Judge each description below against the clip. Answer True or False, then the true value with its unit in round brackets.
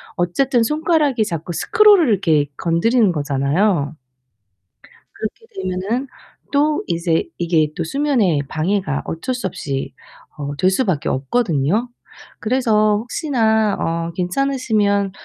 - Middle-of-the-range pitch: False (200 Hz)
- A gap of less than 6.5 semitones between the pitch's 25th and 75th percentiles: False (7.1 semitones)